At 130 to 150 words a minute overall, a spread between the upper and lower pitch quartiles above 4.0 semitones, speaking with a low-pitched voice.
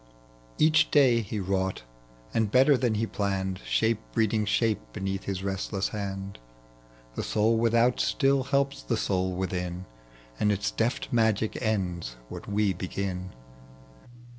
No: slow, 135 wpm; average, 3.3 semitones; low, 105 Hz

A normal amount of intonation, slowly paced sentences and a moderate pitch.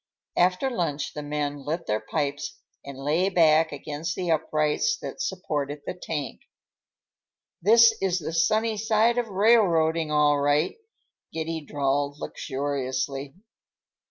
Yes: average, 4.1 semitones; slow, 125 wpm; medium, 155 Hz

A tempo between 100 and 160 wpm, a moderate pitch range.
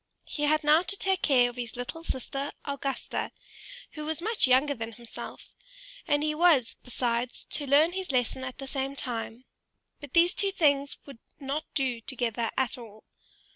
No: average, 175 wpm; average, 3.7 semitones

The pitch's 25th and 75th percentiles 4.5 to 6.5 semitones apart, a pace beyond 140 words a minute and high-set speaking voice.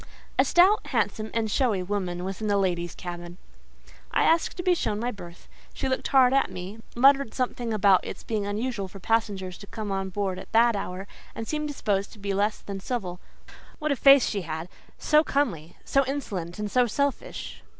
Yes: average, 5.3 semitones; average, 190 wpm; high, 210 Hz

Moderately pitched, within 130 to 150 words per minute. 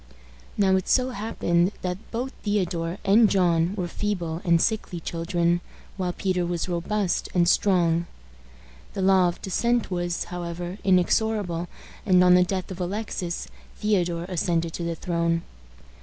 Yes: medium, 180 Hz; average, 140 wpm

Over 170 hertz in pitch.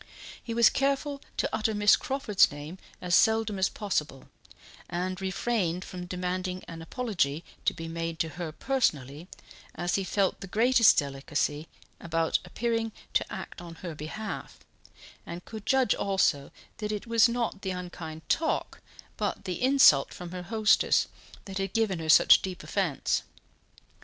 Yes: medium, 185 Hz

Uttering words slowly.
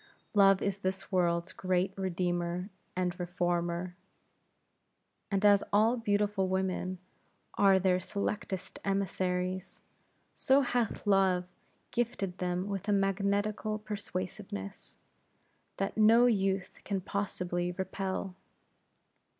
Yes: slow, 100 wpm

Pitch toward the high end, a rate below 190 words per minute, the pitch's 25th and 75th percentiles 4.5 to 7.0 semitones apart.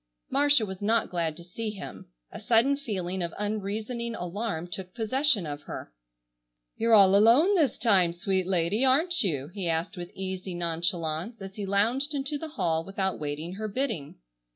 Yes: high, 195 Hz; average, 170 wpm; average, 4.9 semitones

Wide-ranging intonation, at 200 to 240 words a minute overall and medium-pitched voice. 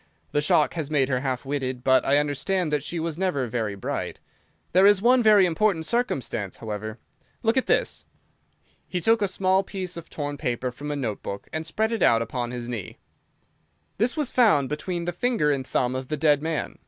Yes: wide, 6.6 semitones; fast, 205 wpm; medium, 150 Hz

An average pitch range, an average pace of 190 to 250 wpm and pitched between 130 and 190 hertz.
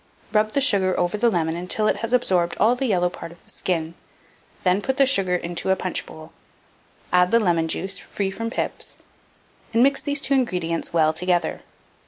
Yes: average, 4.8 semitones; average, 200 wpm; medium, 185 Hz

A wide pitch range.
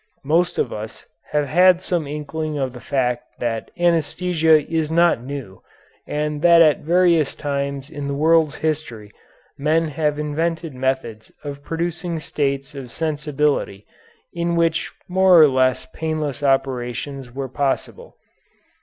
No: average, 3.2 semitones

